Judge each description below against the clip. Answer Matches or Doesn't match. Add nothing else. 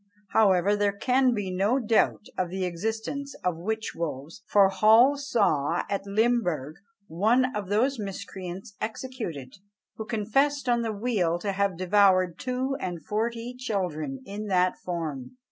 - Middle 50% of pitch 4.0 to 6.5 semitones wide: Matches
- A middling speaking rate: Matches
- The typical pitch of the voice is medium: Doesn't match